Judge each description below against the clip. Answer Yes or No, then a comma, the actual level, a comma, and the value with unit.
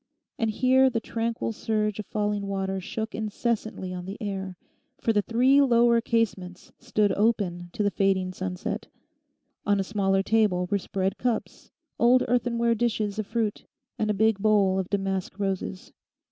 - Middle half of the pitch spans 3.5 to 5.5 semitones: No, average, 2.9 semitones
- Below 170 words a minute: Yes, average, 160 wpm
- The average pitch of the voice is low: No, high, 210 Hz